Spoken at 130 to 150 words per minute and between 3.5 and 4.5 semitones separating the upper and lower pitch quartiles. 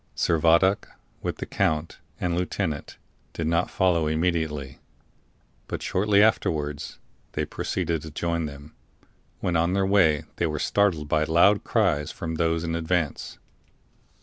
No: slow, 135 wpm; average, 2.7 semitones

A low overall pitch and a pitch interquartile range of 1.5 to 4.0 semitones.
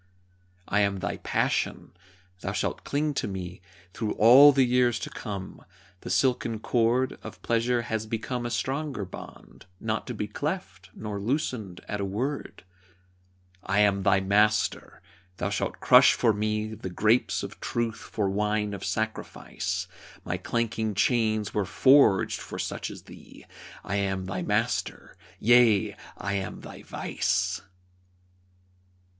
Yes: low, 105 Hz; average, 3.4 semitones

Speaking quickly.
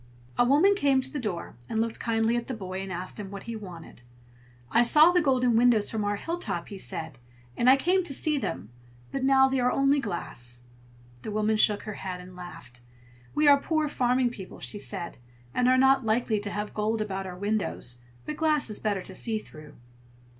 Yes: fast, 210 wpm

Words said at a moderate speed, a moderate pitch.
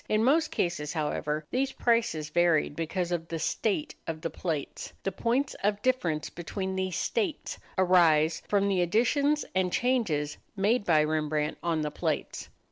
Yes: average, 155 wpm; medium, 180 Hz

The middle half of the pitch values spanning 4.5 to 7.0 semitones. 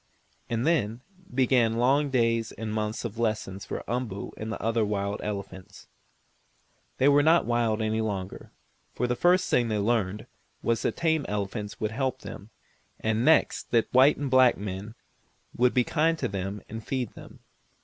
No: average, 3.5 semitones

